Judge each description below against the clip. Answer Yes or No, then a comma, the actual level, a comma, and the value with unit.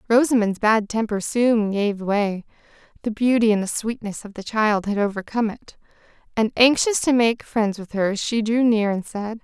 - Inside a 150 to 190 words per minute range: Yes, average, 180 wpm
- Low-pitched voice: No, high, 220 Hz